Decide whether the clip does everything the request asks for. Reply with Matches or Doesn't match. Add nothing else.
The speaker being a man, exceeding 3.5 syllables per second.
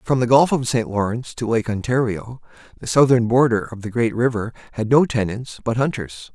Matches